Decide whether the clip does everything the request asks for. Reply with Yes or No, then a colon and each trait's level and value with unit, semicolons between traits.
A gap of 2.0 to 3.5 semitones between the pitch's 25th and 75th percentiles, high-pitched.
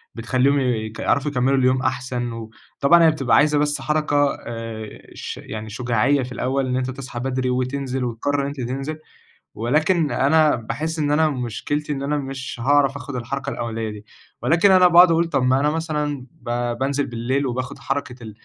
No: average, 2.9 semitones; low, 135 Hz